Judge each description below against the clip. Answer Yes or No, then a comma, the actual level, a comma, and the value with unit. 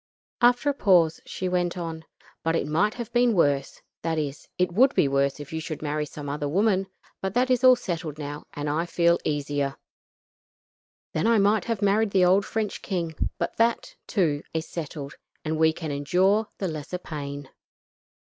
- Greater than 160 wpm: Yes, average, 185 wpm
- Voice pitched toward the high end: No, medium, 170 Hz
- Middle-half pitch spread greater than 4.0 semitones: Yes, average, 5.3 semitones